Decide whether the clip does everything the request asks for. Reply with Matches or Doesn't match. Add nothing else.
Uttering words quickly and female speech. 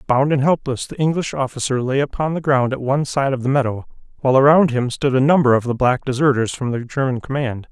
Doesn't match